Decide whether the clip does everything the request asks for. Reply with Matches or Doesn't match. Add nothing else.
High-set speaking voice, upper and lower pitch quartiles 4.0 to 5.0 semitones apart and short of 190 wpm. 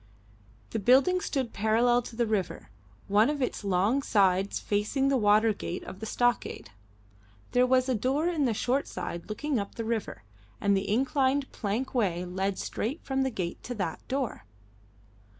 Matches